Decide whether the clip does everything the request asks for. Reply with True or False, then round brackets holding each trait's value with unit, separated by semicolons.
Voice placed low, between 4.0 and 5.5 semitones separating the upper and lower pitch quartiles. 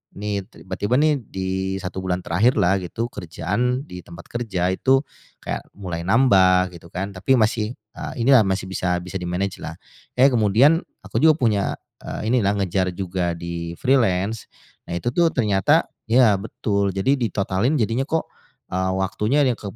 True (100 Hz; 4.7 semitones)